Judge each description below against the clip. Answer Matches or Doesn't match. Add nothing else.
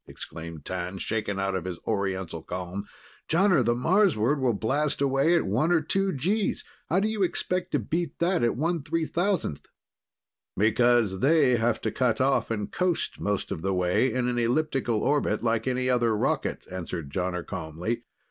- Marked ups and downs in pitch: Matches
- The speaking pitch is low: Matches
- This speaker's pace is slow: Doesn't match